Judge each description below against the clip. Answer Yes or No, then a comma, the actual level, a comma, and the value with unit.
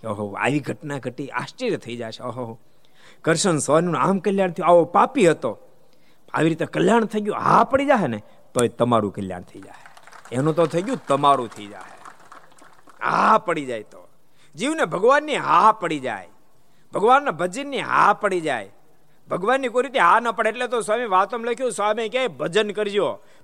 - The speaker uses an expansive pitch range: Yes, wide, 8.6 semitones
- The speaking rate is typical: No, fast, 170 wpm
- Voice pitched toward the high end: No, medium, 175 Hz